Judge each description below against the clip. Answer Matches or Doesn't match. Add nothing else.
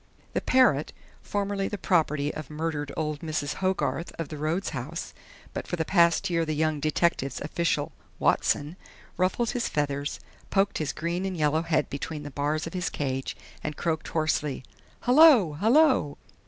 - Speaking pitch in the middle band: Matches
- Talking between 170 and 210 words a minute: Doesn't match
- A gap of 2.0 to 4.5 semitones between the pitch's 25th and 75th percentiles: Matches